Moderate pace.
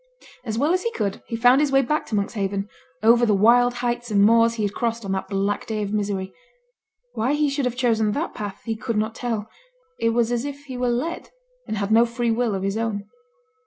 No: fast, 235 wpm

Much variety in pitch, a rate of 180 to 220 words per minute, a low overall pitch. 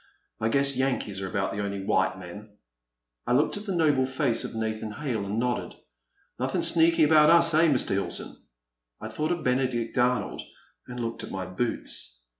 Yes: wide, 5.8 semitones; average, 190 wpm; low, 120 Hz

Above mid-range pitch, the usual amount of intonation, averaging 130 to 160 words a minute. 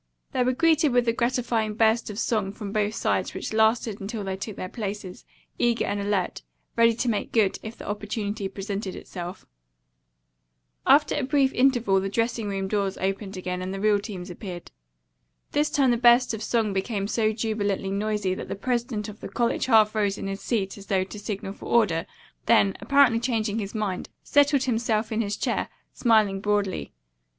No: high, 215 Hz; average, 3.1 semitones; average, 185 wpm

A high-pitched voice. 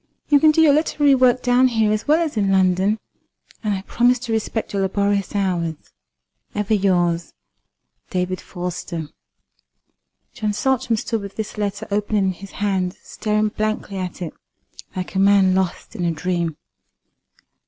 Yes: high, 200 Hz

